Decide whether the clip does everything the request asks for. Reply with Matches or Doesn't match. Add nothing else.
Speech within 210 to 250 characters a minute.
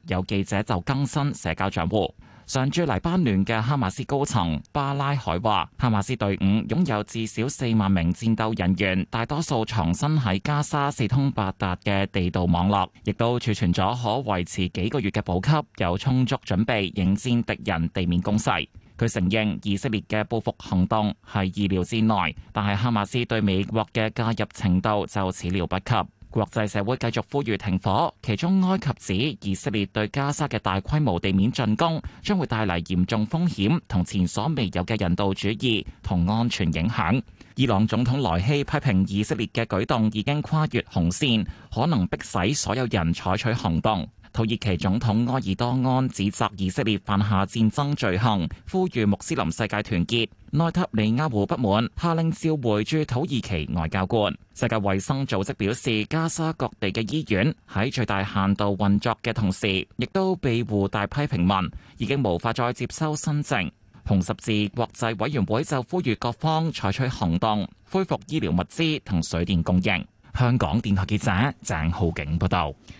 Doesn't match